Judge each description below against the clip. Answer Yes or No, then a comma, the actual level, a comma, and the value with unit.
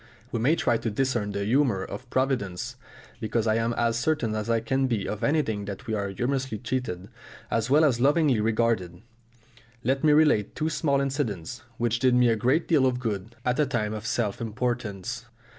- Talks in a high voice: No, low, 120 Hz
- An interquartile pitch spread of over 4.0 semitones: No, average, 3.6 semitones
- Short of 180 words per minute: No, average, 190 wpm